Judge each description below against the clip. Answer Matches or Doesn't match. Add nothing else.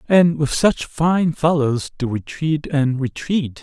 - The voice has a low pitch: Doesn't match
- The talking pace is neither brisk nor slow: Matches